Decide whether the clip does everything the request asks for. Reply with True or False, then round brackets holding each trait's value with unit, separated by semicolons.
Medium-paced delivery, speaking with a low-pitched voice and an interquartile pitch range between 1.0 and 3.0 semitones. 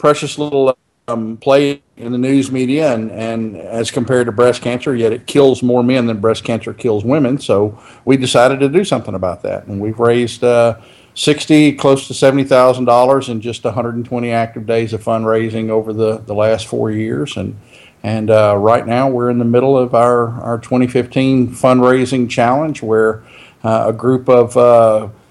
True (190 wpm; 120 Hz; 2.4 semitones)